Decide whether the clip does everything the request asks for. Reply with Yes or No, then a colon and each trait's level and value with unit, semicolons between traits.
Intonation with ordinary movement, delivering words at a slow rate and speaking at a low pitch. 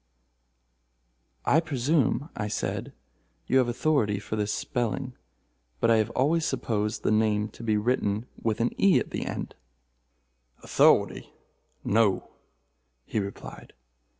Yes: average, 3.9 semitones; slow, 125 wpm; low, 115 Hz